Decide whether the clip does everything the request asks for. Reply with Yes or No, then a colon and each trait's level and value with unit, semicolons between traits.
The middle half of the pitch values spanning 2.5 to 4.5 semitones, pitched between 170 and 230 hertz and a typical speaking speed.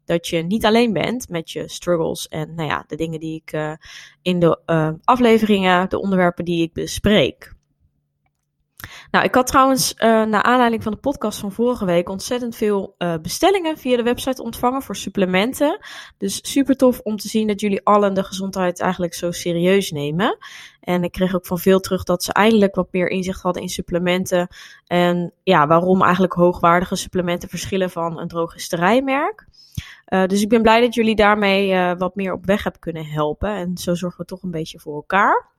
Yes: average, 3.9 semitones; medium, 185 Hz; average, 190 wpm